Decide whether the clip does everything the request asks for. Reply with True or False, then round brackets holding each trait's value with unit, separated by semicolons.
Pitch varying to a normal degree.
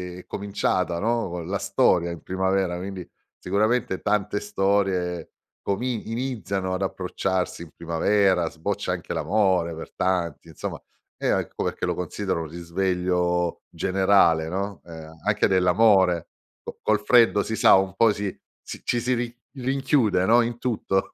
True (3.0 semitones)